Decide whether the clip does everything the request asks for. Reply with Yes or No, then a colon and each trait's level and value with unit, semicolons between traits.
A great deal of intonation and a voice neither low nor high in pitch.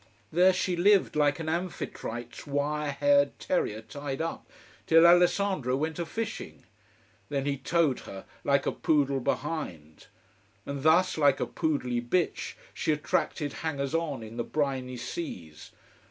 No: average, 4.0 semitones; medium, 145 Hz